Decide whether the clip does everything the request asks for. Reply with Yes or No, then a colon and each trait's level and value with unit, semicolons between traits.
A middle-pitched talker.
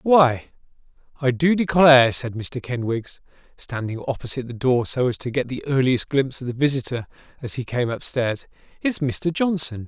No: low, 130 Hz